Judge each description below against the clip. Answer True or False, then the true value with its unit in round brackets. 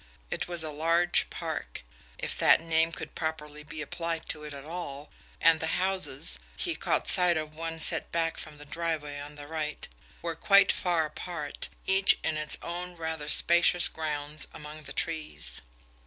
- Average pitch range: False (2.1 semitones)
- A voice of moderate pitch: True (160 Hz)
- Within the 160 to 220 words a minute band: True (170 wpm)